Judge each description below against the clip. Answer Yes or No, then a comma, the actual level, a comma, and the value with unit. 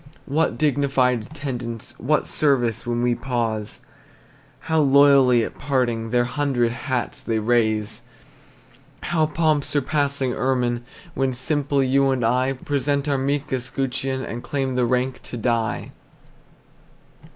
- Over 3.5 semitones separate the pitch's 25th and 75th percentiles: No, average, 2.7 semitones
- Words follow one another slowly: Yes, slow, 130 wpm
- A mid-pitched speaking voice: No, low, 130 Hz